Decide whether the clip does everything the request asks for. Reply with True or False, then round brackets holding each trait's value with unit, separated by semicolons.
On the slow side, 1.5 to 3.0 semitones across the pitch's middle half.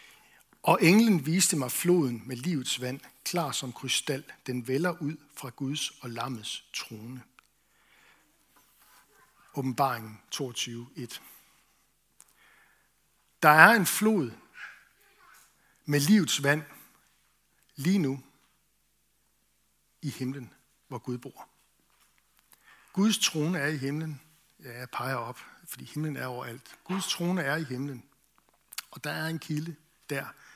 False (115 wpm; 4.3 semitones)